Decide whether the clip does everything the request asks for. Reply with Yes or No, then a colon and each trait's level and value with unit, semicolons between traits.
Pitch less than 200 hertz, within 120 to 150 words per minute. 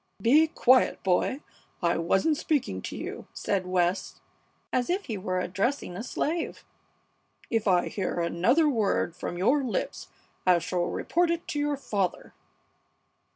No: high, 215 Hz; average, 145 wpm